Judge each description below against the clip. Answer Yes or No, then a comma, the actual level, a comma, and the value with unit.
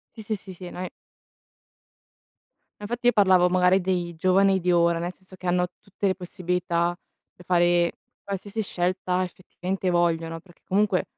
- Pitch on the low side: No, medium, 180 Hz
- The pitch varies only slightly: Yes, narrow, 1.6 semitones